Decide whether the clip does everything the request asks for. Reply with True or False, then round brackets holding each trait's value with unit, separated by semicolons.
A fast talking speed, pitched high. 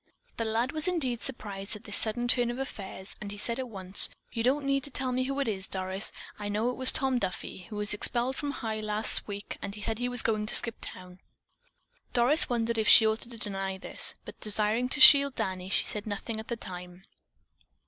True (230 wpm; 220 Hz)